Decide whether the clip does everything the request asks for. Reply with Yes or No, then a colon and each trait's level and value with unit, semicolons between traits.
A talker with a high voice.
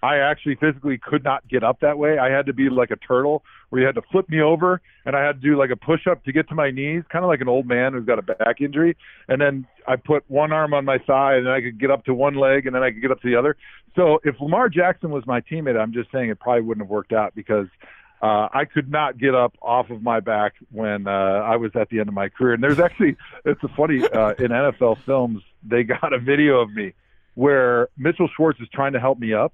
No: low, 135 Hz